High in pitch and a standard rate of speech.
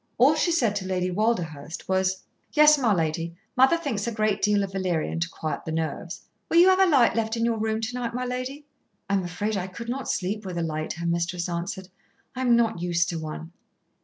No: high, 200 Hz; fast, 225 wpm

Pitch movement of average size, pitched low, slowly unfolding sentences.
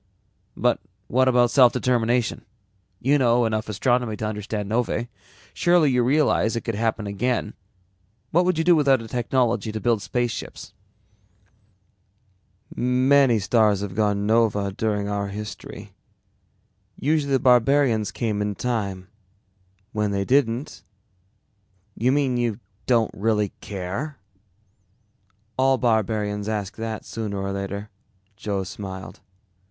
Yes: average, 3.4 semitones; low, 115 Hz; slow, 125 wpm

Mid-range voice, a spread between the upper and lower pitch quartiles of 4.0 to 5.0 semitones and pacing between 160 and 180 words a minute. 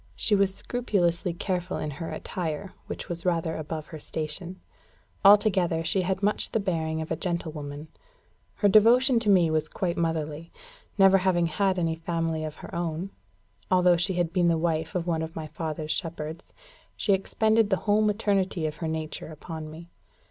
No: medium, 170 Hz; average, 3.2 semitones; average, 175 wpm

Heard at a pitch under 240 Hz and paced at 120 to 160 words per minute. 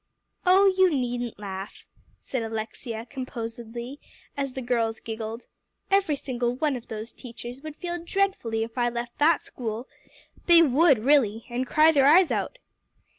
No: very high, 250 Hz; average, 150 wpm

